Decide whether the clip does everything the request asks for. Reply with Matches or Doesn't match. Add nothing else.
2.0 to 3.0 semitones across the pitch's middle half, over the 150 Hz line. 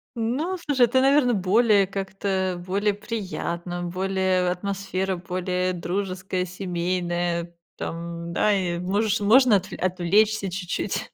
Matches